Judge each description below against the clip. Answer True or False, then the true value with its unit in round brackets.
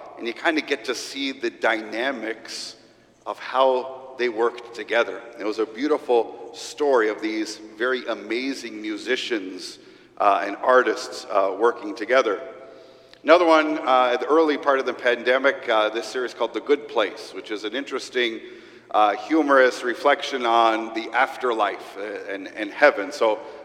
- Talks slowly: False (155 wpm)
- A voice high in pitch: False (165 Hz)